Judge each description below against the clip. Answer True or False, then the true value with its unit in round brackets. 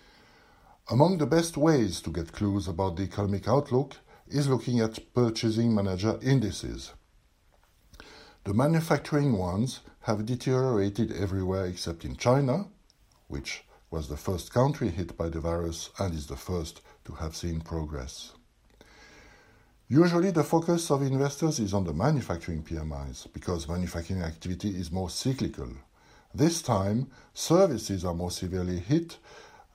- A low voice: True (100 Hz)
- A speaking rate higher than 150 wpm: False (135 wpm)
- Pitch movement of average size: False (7.3 semitones)